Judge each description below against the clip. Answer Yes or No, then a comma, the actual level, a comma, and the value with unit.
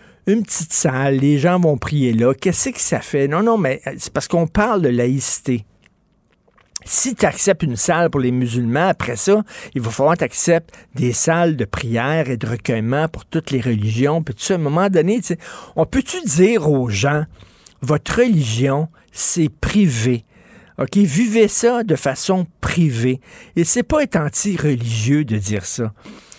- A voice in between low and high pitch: Yes, medium, 155 Hz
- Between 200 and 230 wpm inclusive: No, average, 175 wpm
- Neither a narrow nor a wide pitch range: No, wide, 6.8 semitones